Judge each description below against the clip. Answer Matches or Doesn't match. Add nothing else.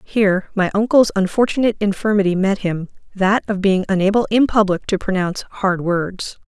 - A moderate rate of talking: Matches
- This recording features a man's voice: Doesn't match